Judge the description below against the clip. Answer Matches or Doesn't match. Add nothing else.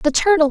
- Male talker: Doesn't match